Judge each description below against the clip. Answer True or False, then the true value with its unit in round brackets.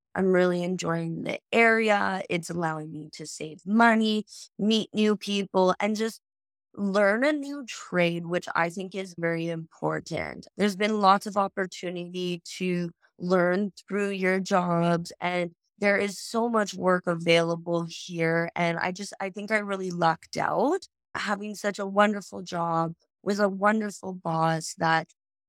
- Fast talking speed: False (150 wpm)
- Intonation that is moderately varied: True (3.3 semitones)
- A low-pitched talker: False (185 Hz)